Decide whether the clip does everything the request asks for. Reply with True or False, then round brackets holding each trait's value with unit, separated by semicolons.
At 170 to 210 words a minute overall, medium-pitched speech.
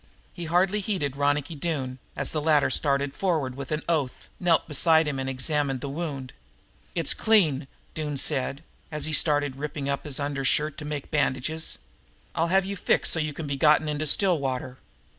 True (180 wpm; 150 Hz)